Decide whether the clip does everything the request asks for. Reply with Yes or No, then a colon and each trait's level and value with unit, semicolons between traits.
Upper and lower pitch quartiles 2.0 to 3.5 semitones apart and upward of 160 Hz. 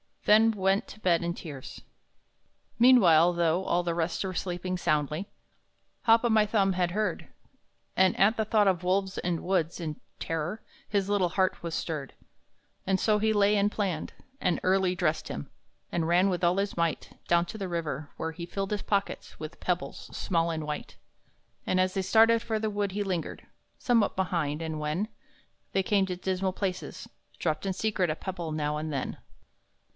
Yes: average, 3.2 semitones; medium, 185 Hz